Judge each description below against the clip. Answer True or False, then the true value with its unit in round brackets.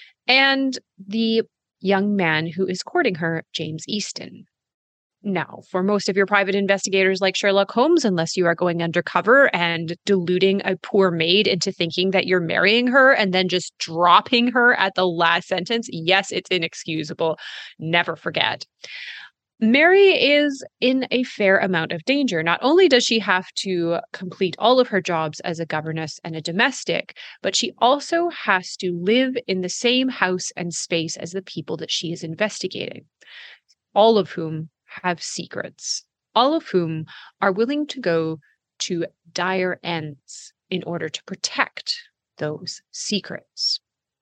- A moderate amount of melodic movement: True (4.9 semitones)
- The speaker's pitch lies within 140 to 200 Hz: True (185 Hz)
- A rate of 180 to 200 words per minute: False (155 wpm)